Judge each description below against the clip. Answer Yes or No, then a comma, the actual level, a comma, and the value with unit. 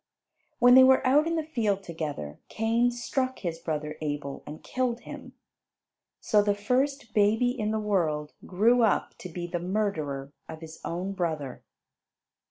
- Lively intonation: Yes, wide, 7.3 semitones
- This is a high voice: Yes, high, 205 Hz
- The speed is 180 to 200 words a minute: No, average, 160 wpm